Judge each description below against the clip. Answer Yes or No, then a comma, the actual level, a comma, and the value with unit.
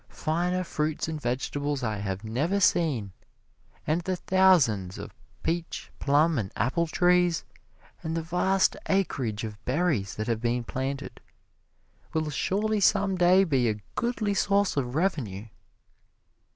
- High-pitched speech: No, medium, 155 Hz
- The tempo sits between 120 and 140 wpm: Yes, slow, 135 wpm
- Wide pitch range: Yes, wide, 7.0 semitones